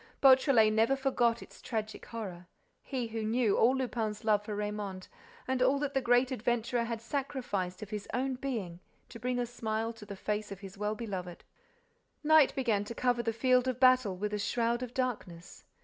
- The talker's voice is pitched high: Yes, high, 230 Hz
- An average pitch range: Yes, average, 3.4 semitones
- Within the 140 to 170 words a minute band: No, average, 190 wpm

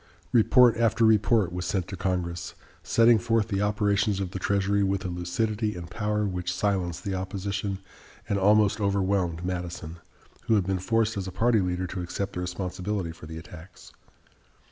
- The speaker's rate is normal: Yes, average, 170 wpm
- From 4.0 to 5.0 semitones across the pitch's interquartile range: No, average, 2.8 semitones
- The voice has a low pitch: Yes, very low, 95 Hz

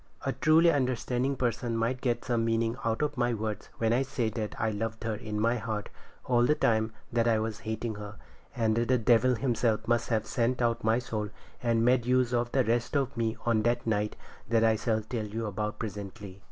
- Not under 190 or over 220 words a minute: Yes, fast, 205 wpm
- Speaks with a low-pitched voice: Yes, low, 115 Hz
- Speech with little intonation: Yes, narrow, 1.8 semitones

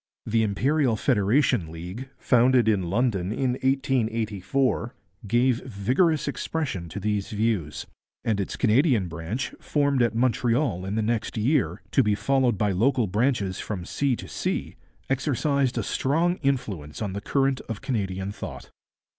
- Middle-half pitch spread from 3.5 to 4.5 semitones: No, average, 4.9 semitones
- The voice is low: Yes, low, 115 Hz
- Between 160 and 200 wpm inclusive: No, average, 145 wpm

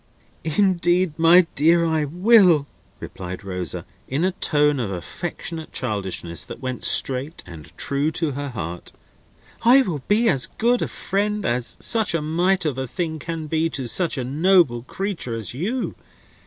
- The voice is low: No, medium, 155 Hz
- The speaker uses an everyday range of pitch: No, wide, 6.2 semitones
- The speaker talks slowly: No, average, 160 wpm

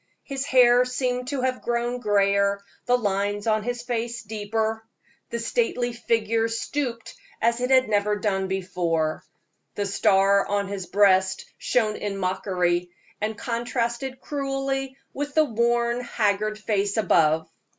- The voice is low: No, high, 225 Hz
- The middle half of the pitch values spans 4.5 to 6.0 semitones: No, average, 3.5 semitones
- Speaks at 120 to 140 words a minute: Yes, slow, 135 wpm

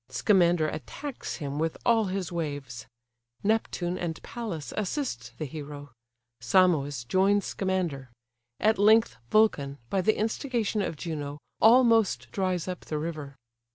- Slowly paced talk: Yes, slow, 125 wpm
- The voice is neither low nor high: Yes, medium, 175 Hz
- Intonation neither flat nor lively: No, wide, 6.5 semitones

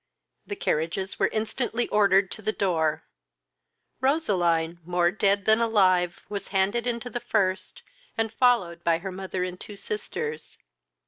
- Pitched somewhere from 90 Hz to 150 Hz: No, high, 195 Hz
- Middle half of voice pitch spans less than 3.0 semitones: No, average, 3.8 semitones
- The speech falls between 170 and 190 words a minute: No, average, 140 wpm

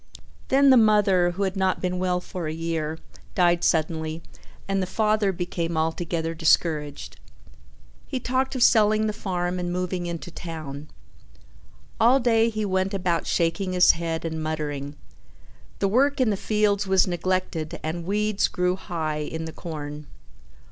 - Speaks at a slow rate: No, average, 155 wpm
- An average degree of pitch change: Yes, average, 3.8 semitones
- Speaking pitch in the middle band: Yes, medium, 180 Hz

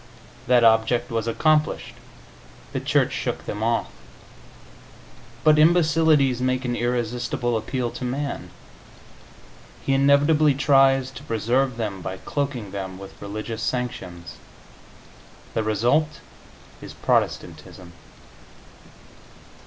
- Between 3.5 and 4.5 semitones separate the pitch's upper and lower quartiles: Yes, average, 4.1 semitones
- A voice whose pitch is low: Yes, low, 125 Hz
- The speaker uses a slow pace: Yes, slow, 100 wpm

